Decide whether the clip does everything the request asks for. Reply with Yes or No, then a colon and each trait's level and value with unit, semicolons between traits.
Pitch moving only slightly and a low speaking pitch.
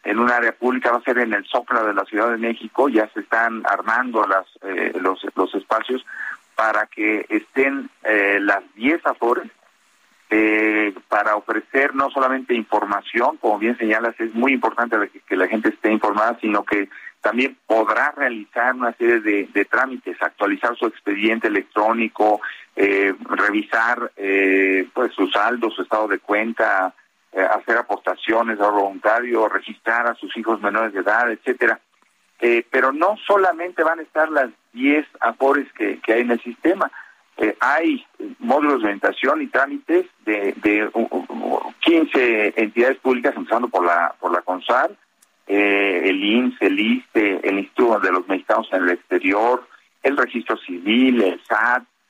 No: average, 4.1 semitones; low, 115 Hz